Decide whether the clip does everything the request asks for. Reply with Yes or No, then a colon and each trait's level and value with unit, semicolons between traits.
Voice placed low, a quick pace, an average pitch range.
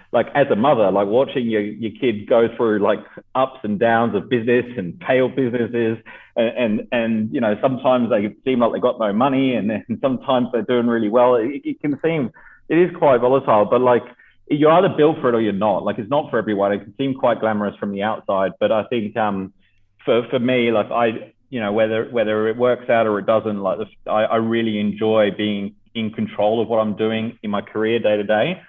Yes: low, 115 Hz; fast, 230 wpm; average, 3.1 semitones